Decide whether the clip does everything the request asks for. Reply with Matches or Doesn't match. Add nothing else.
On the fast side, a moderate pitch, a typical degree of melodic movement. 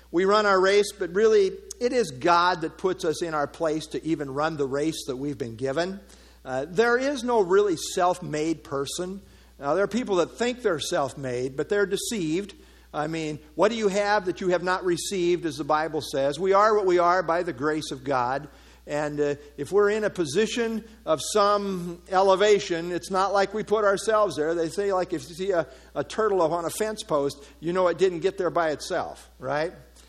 Matches